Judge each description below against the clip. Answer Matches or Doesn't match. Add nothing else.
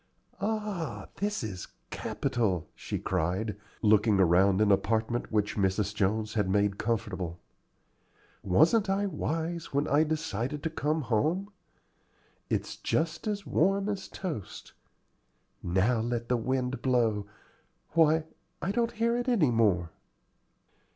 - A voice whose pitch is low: Matches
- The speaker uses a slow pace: Matches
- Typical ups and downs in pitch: Doesn't match